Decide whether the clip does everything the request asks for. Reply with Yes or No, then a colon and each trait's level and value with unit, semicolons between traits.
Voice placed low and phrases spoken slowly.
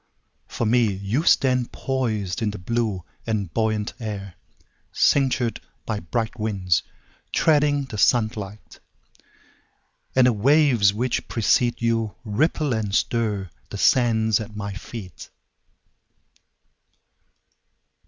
Yes: low, 110 Hz; slow, 85 wpm